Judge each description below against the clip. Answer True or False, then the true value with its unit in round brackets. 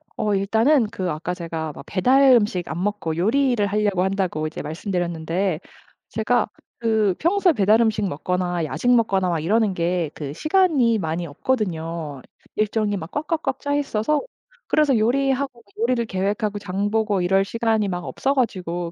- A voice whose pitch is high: True (205 Hz)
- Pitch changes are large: False (4.9 semitones)